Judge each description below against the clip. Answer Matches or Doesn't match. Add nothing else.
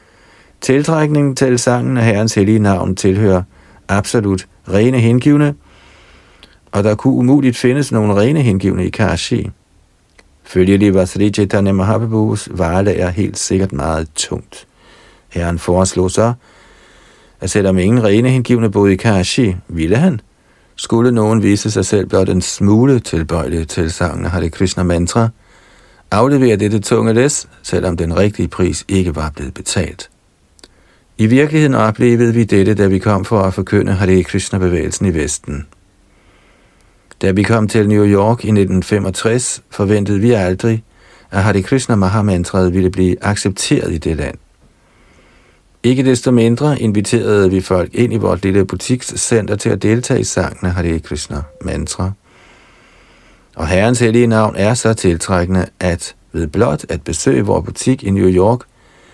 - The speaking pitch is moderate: Doesn't match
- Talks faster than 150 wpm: Doesn't match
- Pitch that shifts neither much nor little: Matches